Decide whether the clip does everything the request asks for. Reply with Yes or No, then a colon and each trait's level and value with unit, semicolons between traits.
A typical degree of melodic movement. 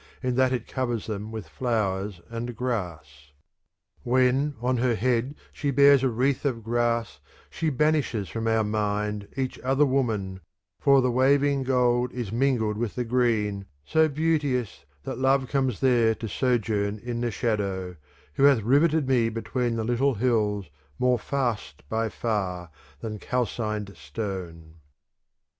Yes: average, 3.7 semitones